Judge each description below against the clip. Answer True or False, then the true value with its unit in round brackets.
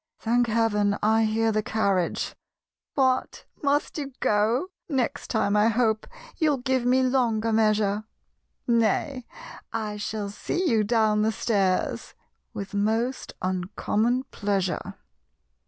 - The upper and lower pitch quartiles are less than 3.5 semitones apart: True (3.1 semitones)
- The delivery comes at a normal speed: False (120 wpm)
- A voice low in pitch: False (220 Hz)